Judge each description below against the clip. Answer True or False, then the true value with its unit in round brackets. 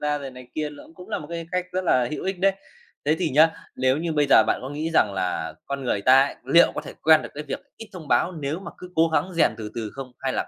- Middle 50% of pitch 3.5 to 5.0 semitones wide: True (4.2 semitones)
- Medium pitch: True (150 Hz)